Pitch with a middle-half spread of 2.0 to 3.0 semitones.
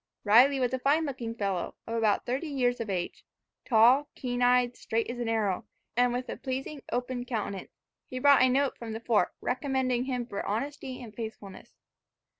Yes: narrow, 2.5 semitones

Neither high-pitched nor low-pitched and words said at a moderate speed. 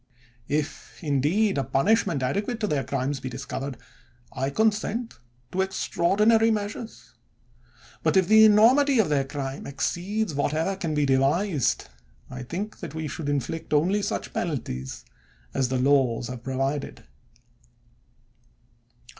No: medium, 155 Hz; slow, 130 wpm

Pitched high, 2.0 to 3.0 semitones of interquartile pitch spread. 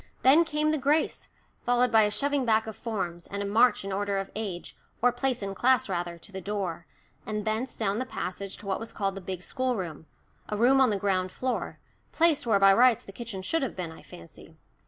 No: high, 210 Hz; average, 4.5 semitones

